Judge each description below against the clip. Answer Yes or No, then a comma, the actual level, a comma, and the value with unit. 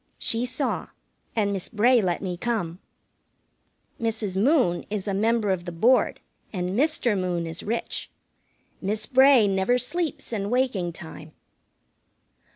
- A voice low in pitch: No, high, 210 Hz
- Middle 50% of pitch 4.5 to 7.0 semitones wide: Yes, average, 4.8 semitones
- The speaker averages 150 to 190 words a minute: No, slow, 135 wpm